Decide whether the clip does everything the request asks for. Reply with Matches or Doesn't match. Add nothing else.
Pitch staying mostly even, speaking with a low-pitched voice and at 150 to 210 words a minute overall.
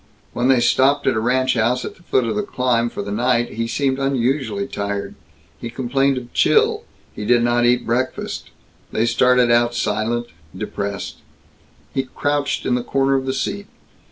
Matches